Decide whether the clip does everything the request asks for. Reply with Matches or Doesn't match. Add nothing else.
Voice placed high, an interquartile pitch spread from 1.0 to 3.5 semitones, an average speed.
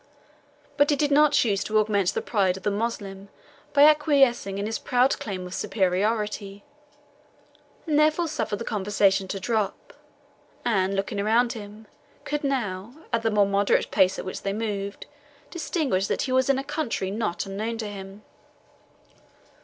Doesn't match